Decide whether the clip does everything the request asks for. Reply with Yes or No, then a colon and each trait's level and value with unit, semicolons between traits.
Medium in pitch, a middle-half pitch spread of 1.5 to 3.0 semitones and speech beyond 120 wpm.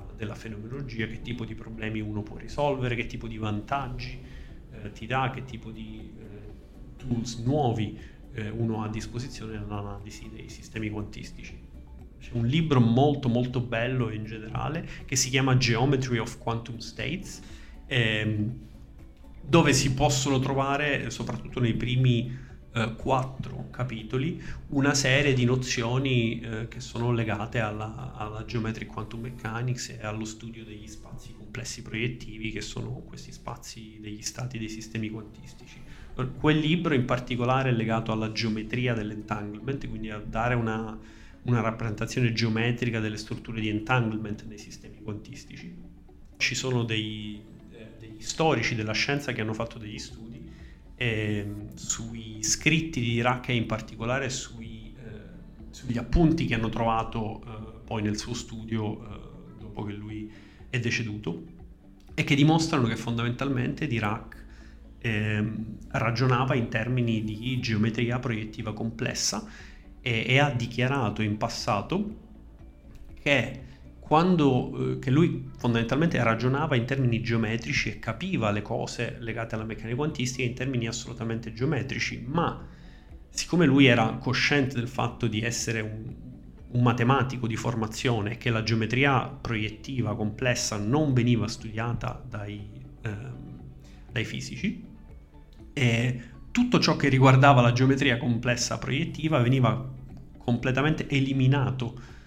No: low, 115 Hz; average, 2.7 semitones; average, 135 wpm